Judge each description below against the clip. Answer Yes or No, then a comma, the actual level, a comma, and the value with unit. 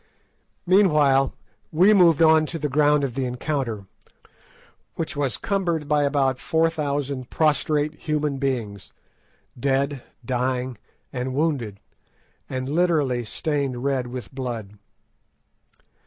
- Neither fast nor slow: No, slow, 110 wpm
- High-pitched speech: No, medium, 140 Hz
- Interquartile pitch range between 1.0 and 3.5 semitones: Yes, average, 3.2 semitones